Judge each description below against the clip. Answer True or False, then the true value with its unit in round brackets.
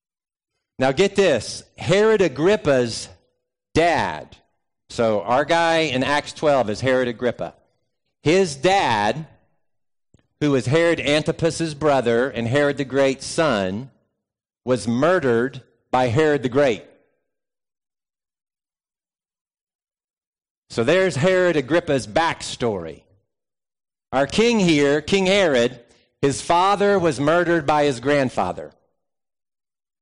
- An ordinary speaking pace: False (100 wpm)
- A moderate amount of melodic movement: True (4.9 semitones)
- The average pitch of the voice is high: False (145 Hz)